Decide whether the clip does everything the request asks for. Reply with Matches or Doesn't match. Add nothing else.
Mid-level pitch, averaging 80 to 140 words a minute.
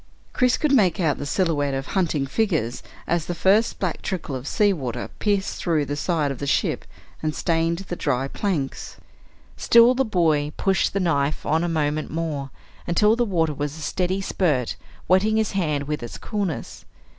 Doesn't match